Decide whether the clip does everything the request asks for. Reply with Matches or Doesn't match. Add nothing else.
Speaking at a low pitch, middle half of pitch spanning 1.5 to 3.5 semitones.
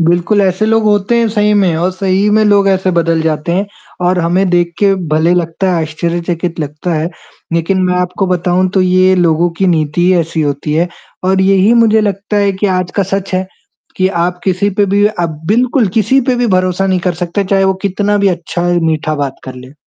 Doesn't match